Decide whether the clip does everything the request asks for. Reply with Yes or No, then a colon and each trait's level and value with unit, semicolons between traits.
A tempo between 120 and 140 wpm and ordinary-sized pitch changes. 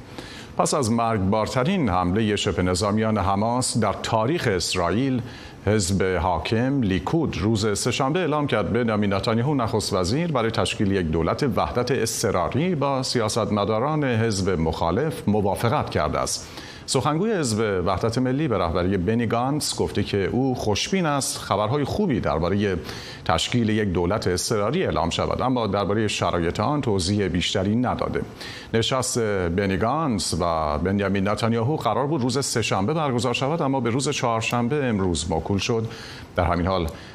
Yes: average, 135 wpm; average, 4.5 semitones